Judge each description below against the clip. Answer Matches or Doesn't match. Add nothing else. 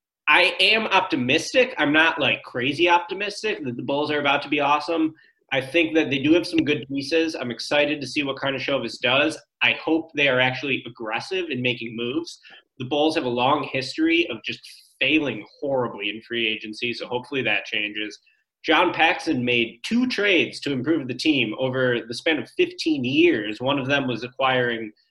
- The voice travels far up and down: Doesn't match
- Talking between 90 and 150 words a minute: Doesn't match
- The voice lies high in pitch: Doesn't match